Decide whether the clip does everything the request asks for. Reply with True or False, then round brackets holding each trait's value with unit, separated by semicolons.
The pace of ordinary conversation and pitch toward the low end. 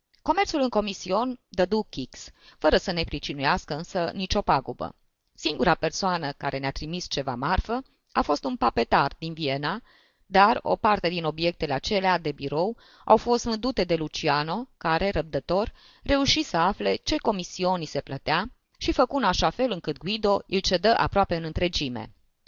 False (155 wpm; 180 Hz)